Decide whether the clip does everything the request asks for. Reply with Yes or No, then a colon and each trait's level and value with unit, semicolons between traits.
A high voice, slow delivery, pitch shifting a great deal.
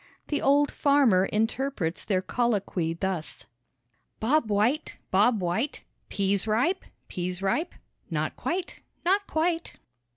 Yes: high, 225 Hz; slow, 110 wpm; wide, 7.3 semitones